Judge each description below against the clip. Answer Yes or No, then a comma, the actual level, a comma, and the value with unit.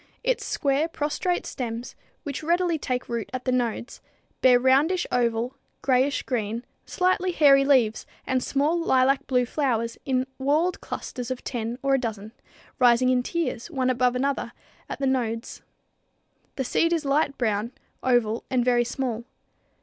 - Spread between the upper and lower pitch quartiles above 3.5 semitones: No, average, 2.9 semitones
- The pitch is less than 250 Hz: No, very high, 255 Hz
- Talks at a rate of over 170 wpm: No, average, 150 wpm